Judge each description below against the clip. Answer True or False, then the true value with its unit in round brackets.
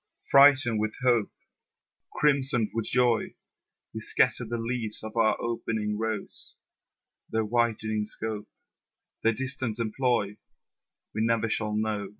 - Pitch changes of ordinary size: False (2.0 semitones)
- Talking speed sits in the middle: False (120 wpm)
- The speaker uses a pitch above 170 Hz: False (115 Hz)